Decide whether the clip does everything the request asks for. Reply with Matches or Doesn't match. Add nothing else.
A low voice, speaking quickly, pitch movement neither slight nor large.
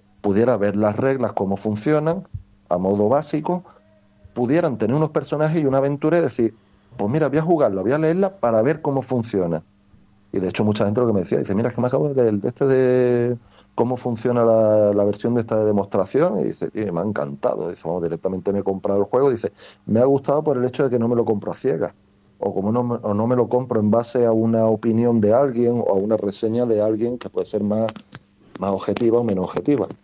Matches